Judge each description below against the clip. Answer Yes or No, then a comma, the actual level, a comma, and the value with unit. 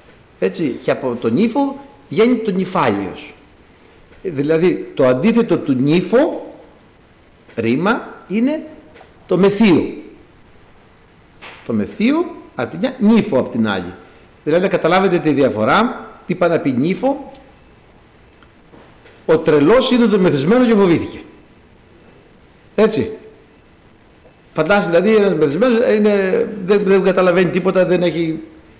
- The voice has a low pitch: No, high, 190 Hz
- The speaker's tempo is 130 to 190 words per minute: No, slow, 115 wpm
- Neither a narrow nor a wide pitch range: No, wide, 6.2 semitones